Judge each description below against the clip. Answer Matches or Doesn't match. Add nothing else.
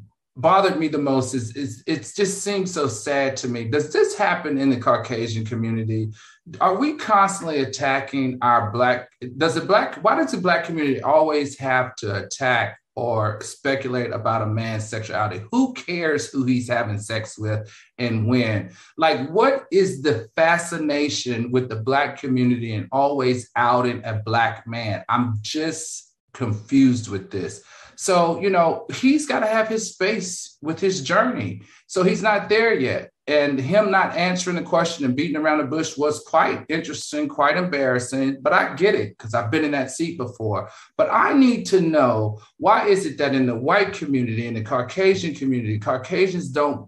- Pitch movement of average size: Doesn't match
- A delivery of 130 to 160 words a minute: Doesn't match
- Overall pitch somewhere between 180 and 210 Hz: Doesn't match